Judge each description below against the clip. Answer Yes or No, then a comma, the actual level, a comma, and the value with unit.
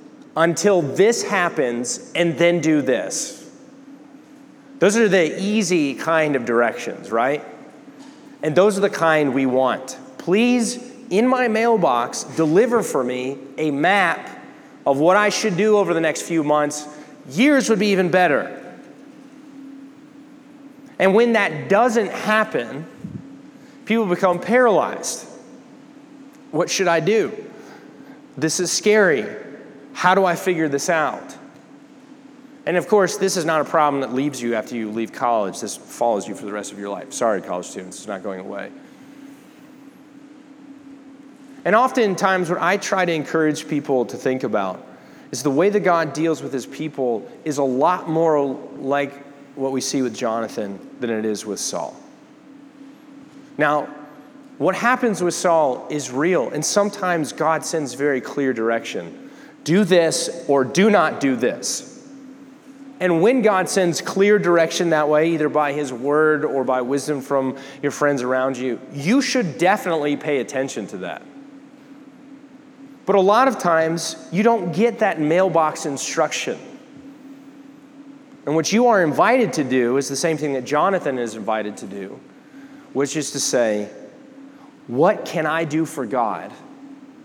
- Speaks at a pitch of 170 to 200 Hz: Yes, medium, 185 Hz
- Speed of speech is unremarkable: Yes, average, 150 wpm